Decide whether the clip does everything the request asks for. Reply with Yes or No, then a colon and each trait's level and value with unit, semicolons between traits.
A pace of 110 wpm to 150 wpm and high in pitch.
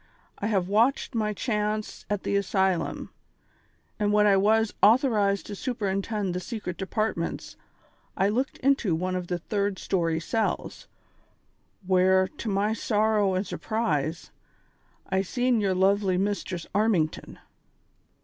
Yes: slow, 135 wpm; high, 200 Hz